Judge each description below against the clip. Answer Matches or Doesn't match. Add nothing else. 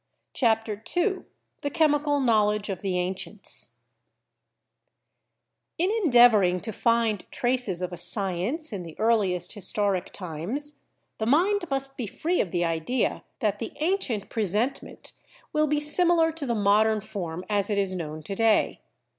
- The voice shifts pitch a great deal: Matches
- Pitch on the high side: Matches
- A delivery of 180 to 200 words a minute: Doesn't match